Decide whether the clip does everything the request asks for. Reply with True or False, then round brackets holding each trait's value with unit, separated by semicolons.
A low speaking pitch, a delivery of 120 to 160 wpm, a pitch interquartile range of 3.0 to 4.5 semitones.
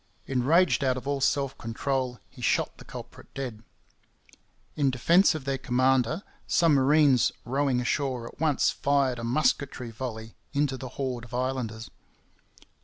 False (130 Hz; 145 wpm; 2.4 semitones)